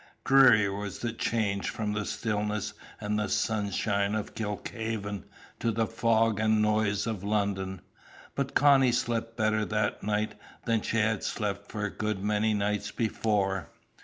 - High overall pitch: No, low, 105 Hz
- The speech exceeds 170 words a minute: No, average, 145 wpm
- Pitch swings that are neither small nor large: No, narrow, 1.6 semitones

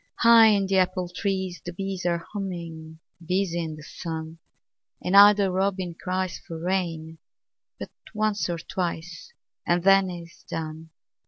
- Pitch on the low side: No, medium, 180 Hz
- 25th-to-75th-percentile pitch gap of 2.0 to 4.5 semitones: Yes, average, 2.7 semitones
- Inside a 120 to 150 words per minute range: Yes, average, 145 wpm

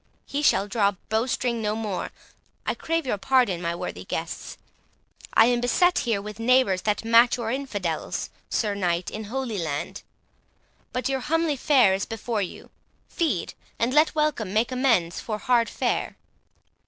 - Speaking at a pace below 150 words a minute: No, average, 155 wpm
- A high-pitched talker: Yes, high, 230 Hz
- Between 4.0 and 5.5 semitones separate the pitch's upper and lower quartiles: Yes, average, 4.3 semitones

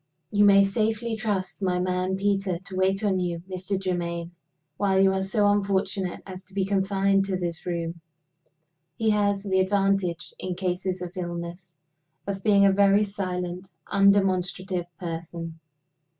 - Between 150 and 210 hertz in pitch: Yes, high, 190 Hz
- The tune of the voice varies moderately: No, narrow, 1.7 semitones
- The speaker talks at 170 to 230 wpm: No, average, 150 wpm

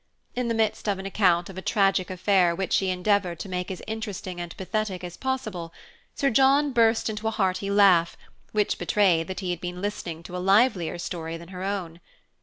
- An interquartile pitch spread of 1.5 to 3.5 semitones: Yes, average, 3.2 semitones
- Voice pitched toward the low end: No, high, 190 Hz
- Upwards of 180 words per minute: Yes, fast, 205 wpm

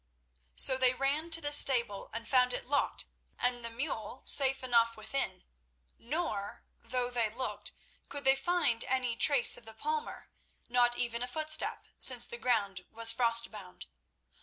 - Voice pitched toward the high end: Yes, high, 245 Hz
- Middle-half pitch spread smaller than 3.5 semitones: Yes, average, 2.9 semitones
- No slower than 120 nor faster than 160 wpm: Yes, average, 140 wpm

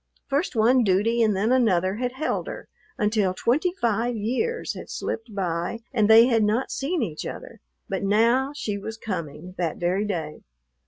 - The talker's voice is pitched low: No, high, 220 Hz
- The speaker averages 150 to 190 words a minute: Yes, average, 170 wpm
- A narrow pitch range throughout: No, average, 4.2 semitones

